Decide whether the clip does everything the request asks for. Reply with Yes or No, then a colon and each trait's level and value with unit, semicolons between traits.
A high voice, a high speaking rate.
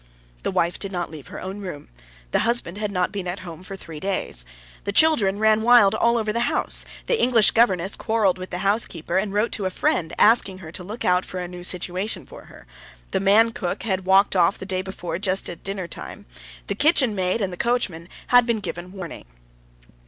Yes: high, 195 Hz; fast, 210 wpm